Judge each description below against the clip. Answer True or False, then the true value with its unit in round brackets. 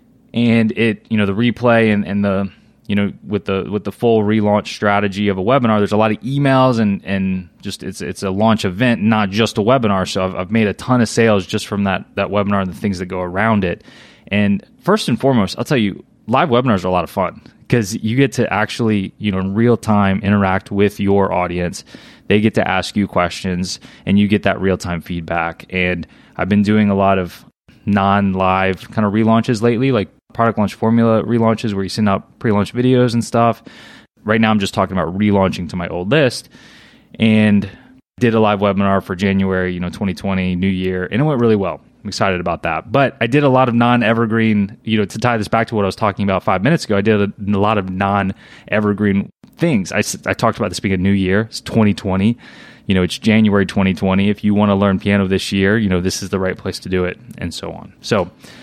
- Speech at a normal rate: False (235 wpm)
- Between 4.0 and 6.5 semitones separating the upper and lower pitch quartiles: False (2.7 semitones)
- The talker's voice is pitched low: True (100 Hz)